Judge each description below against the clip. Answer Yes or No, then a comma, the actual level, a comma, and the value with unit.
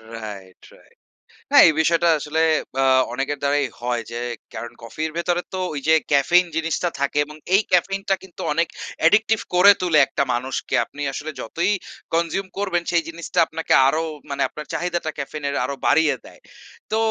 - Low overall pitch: No, medium, 160 Hz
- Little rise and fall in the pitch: No, average, 3.9 semitones